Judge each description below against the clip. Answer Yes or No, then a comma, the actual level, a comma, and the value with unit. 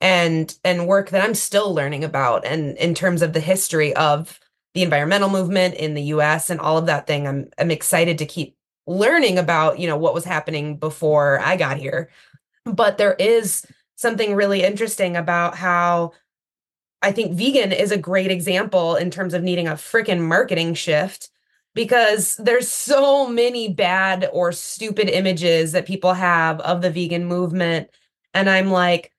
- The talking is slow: No, average, 170 wpm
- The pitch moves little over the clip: No, average, 3.0 semitones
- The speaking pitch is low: No, medium, 180 Hz